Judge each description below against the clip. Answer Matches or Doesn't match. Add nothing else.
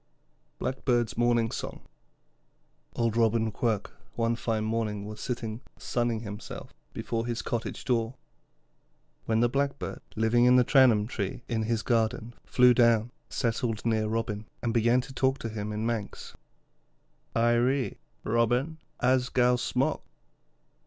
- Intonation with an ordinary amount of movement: Doesn't match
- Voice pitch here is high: Doesn't match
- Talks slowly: Matches